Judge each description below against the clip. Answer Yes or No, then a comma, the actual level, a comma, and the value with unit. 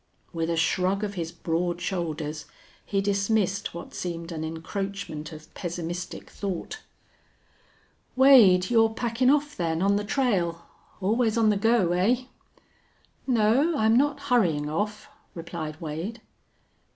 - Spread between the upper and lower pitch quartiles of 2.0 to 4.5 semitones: No, average, 5.1 semitones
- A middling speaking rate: No, slow, 125 wpm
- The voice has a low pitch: No, high, 195 Hz